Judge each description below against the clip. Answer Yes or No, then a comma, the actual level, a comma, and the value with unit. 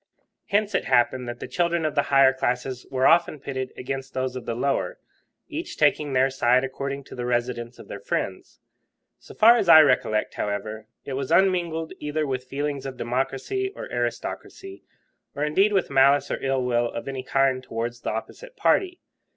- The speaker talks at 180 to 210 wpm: Yes, average, 185 wpm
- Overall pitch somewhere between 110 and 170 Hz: Yes, low, 135 Hz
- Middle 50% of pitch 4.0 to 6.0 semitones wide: No, average, 3.5 semitones